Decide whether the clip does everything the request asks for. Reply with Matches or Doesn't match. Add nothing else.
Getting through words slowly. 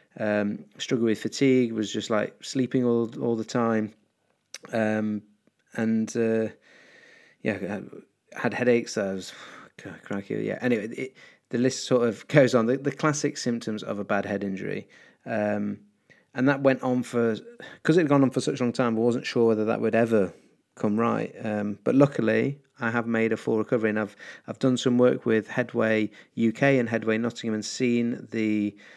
Doesn't match